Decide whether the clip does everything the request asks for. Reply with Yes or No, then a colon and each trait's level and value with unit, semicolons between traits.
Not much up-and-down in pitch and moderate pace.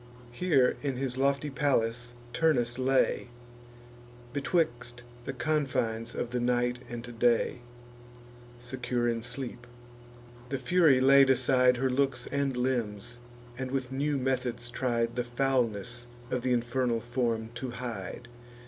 No: narrow, 1.9 semitones; slow, 125 wpm